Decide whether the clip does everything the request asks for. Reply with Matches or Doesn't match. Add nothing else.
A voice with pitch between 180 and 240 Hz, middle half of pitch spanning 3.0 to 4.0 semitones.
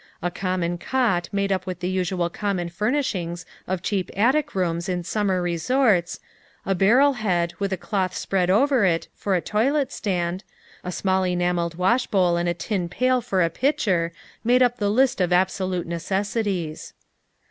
Matches